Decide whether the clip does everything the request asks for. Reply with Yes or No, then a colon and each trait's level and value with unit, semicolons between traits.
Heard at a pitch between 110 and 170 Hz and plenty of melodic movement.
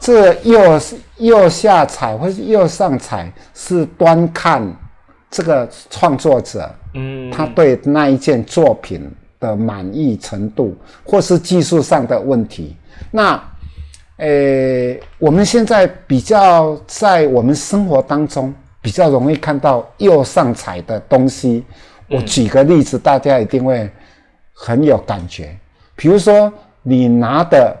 Yes: low, 135 Hz; wide, 7.5 semitones